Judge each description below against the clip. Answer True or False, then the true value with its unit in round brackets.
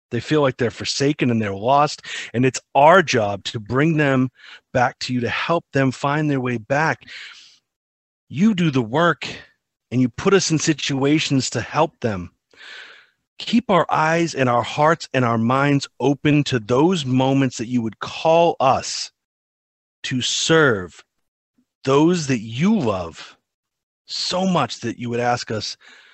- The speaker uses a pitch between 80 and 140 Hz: True (135 Hz)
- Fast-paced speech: False (160 wpm)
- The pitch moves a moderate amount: True (4.5 semitones)